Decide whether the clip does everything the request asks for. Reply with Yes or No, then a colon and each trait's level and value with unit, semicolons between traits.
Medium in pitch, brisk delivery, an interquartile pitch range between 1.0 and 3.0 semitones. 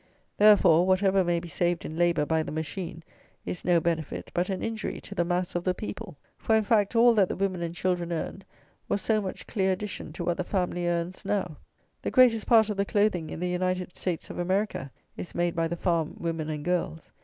Yes: medium, 180 Hz; fast, 220 wpm; average, 2.7 semitones